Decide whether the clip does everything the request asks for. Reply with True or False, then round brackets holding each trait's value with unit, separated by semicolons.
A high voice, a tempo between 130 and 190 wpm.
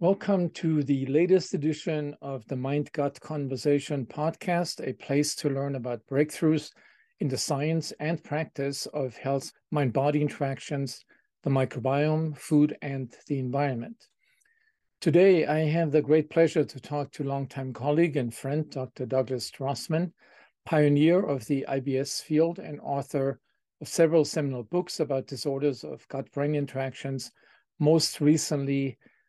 False (145 Hz; 135 wpm)